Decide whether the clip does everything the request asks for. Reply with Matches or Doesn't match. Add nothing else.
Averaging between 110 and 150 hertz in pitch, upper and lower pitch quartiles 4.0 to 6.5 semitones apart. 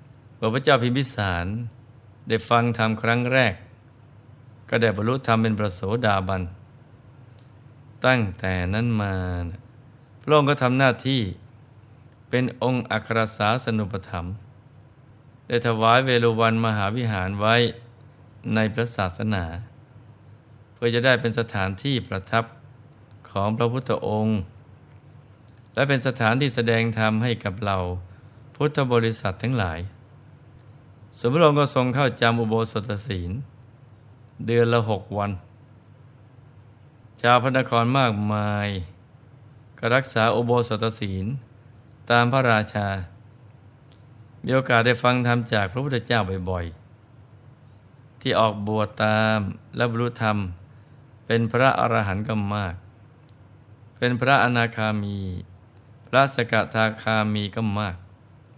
Doesn't match